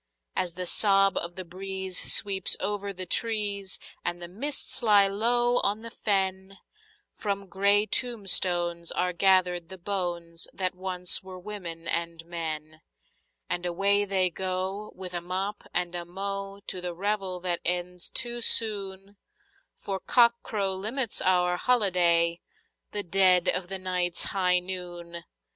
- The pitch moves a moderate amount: No, narrow, 2.2 semitones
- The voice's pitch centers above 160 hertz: Yes, high, 190 Hz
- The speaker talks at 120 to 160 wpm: Yes, average, 140 wpm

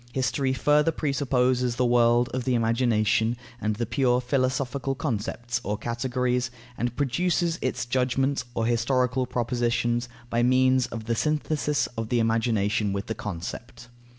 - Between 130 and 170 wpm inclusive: Yes, average, 140 wpm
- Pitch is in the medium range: No, low, 125 Hz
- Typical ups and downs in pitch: No, narrow, 2.0 semitones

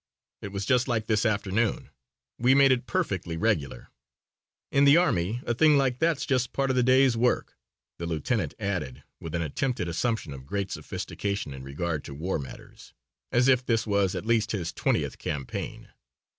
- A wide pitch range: Yes, wide, 6.9 semitones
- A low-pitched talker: Yes, low, 105 Hz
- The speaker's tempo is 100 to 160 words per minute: No, average, 175 wpm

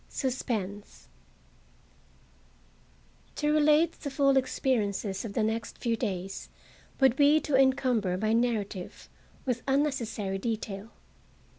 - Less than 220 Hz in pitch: No, high, 235 Hz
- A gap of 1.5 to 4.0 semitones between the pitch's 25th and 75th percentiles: No, average, 4.7 semitones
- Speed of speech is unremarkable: No, slow, 105 wpm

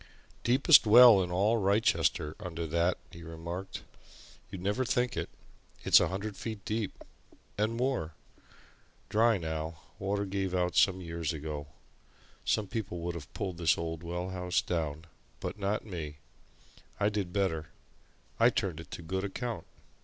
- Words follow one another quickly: No, average, 150 wpm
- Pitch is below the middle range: Yes, very low, 95 Hz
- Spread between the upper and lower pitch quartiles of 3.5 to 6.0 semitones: Yes, average, 4.0 semitones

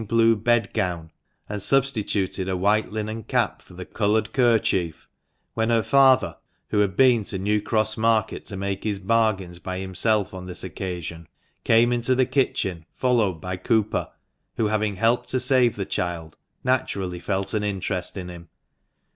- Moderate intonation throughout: Yes, average, 3.5 semitones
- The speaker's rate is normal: Yes, average, 160 wpm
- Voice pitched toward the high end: No, low, 105 Hz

